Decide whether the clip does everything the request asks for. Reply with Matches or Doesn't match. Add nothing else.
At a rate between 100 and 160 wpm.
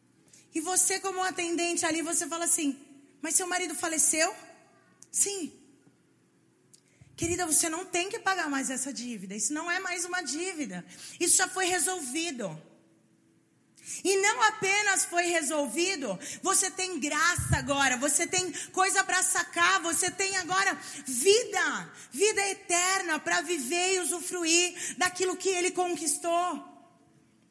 Matches